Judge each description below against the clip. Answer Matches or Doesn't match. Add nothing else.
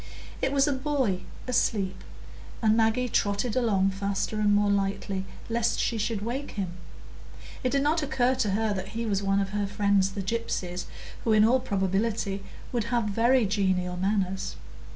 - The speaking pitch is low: Doesn't match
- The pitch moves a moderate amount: Matches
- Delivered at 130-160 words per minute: Doesn't match